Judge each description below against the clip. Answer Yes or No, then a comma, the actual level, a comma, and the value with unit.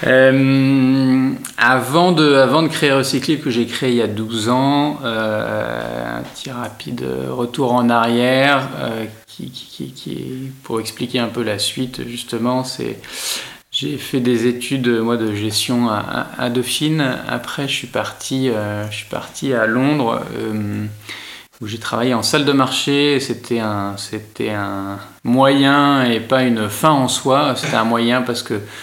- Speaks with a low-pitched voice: Yes, low, 125 Hz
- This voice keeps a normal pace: Yes, average, 165 wpm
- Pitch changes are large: No, average, 3.3 semitones